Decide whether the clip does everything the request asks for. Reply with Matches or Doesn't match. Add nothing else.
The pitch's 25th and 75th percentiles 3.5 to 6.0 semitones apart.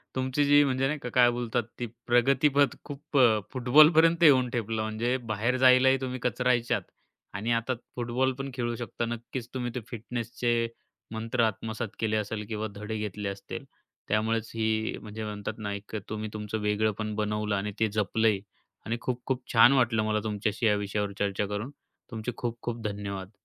Doesn't match